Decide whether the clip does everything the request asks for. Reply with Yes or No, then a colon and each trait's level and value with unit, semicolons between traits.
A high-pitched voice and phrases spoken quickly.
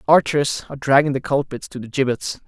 No: low, 135 Hz; fast, 220 wpm